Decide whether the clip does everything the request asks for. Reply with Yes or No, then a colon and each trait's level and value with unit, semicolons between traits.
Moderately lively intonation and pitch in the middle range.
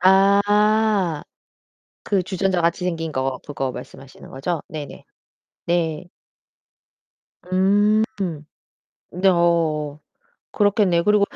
Yes: average, 4.2 semitones; medium, 180 Hz